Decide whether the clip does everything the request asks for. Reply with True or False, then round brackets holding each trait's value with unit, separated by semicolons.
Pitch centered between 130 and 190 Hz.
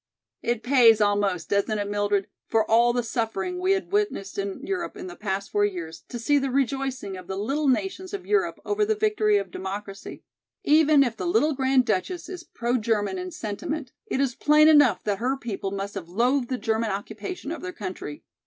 False (240 Hz)